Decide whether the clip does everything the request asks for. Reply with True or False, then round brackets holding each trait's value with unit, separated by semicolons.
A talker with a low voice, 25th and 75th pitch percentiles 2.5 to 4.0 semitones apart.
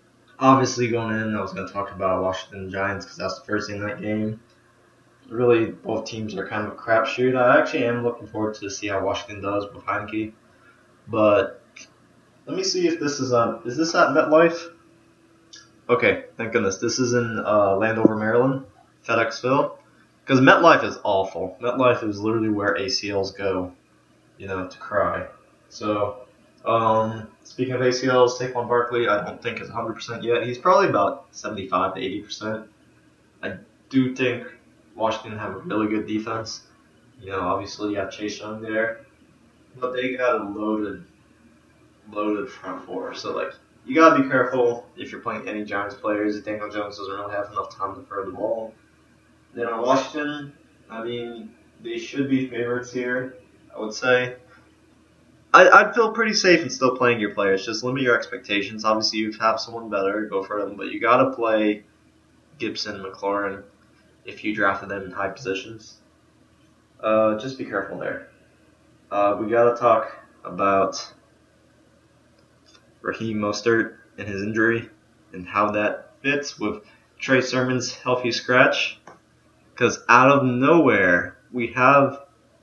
True (110 Hz; 3.4 semitones)